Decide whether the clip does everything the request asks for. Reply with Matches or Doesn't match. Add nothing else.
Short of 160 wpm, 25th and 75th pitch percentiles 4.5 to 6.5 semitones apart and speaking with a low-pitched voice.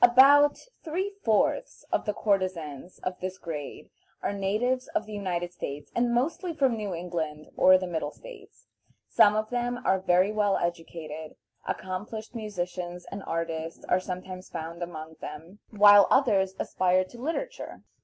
Doesn't match